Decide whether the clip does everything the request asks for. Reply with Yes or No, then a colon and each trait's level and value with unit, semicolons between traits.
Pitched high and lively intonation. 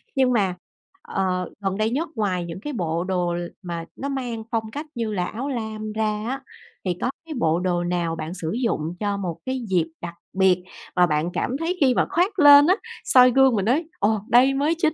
Yes: high, 215 Hz; wide, 6.6 semitones